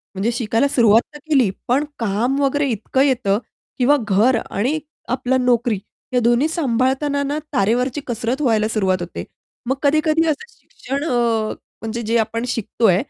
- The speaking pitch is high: Yes, high, 245 Hz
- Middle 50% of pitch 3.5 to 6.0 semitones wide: Yes, average, 3.9 semitones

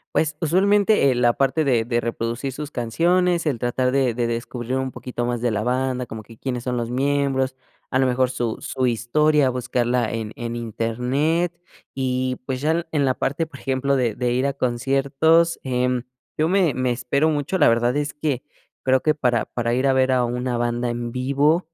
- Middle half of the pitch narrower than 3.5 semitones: Yes, average, 2.9 semitones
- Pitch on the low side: Yes, low, 130 Hz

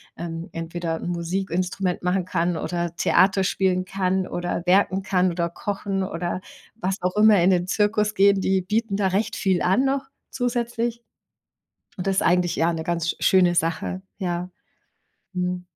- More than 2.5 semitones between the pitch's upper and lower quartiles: No, narrow, 2.1 semitones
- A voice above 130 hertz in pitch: Yes, medium, 185 Hz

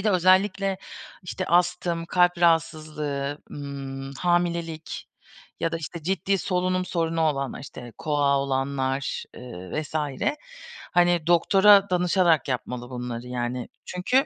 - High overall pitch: No, medium, 165 Hz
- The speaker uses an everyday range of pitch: Yes, average, 4.6 semitones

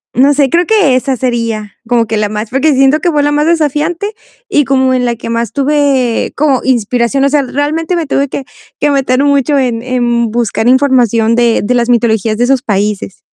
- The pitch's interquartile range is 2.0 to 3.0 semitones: No, average, 3.5 semitones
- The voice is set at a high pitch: Yes, very high, 260 Hz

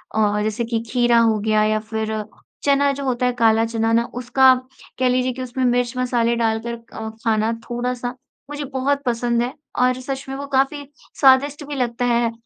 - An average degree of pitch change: No, narrow, 2.3 semitones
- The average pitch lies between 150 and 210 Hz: No, high, 245 Hz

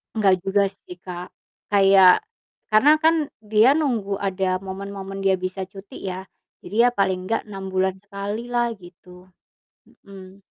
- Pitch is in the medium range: No, high, 195 Hz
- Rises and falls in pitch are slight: Yes, narrow, 1.4 semitones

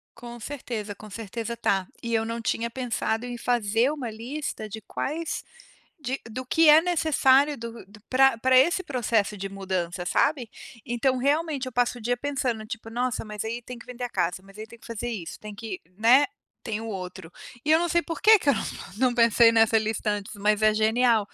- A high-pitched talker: Yes, high, 235 Hz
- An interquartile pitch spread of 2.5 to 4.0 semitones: Yes, average, 3.2 semitones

